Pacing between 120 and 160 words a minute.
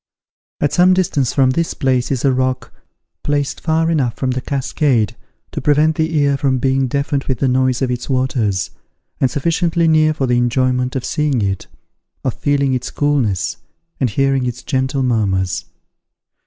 No: average, 170 wpm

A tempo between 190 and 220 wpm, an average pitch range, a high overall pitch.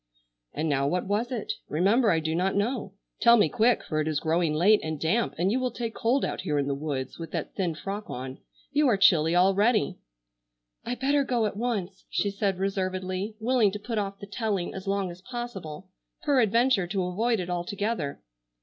Yes: average, 200 wpm; average, 4.8 semitones; high, 195 Hz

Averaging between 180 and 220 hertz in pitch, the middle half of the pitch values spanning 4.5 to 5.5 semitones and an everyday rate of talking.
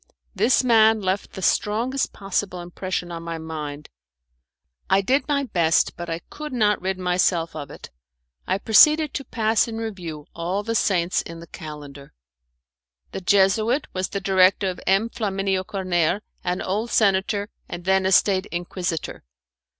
No: high, 190 Hz; average, 3.7 semitones; average, 155 wpm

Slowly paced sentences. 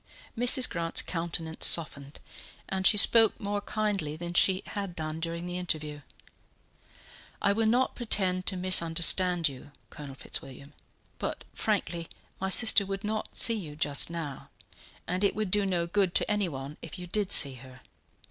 No: average, 155 wpm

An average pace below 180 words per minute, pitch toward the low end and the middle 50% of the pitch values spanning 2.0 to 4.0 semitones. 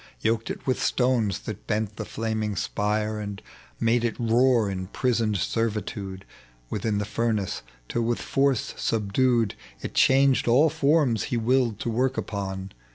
Yes: average, 150 wpm; low, 115 Hz; average, 2.9 semitones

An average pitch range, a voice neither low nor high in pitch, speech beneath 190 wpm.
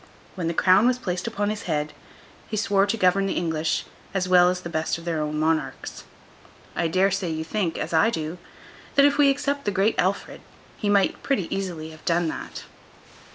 No: average, 4.0 semitones; medium, 180 Hz; average, 200 wpm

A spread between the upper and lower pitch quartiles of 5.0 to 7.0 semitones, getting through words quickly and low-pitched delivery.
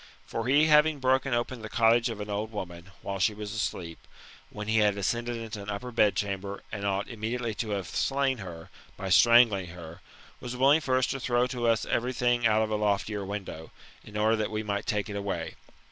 No: average, 3.2 semitones; fast, 220 wpm; low, 110 Hz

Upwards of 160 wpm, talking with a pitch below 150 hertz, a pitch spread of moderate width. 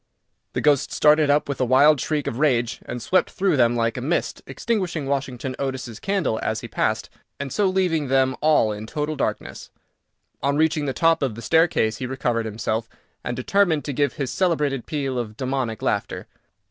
Yes: average, 185 wpm; low, 135 Hz; average, 4.1 semitones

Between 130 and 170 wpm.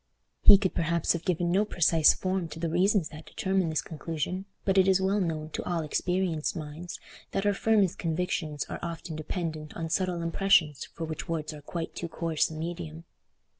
No: average, 190 wpm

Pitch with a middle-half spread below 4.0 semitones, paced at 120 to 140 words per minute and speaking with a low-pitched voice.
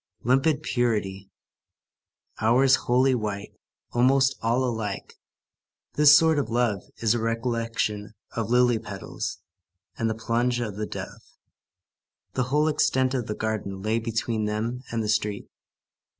Yes: average, 2.9 semitones; slow, 135 wpm; low, 115 Hz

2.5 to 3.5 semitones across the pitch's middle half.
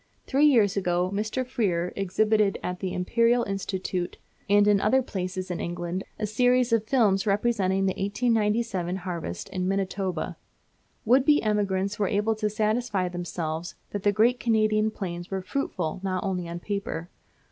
Yes: average, 3.0 semitones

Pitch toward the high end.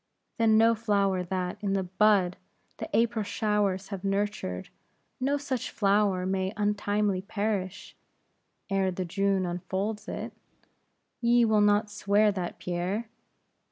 Yes: high, 200 Hz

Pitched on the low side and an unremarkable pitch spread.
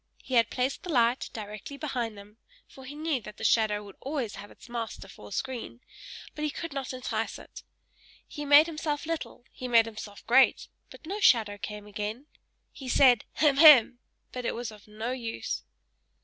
No: high, 245 Hz; average, 4.5 semitones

